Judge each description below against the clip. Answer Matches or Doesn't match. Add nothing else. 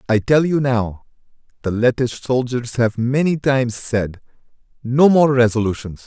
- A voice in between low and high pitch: Doesn't match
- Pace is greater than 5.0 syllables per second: Doesn't match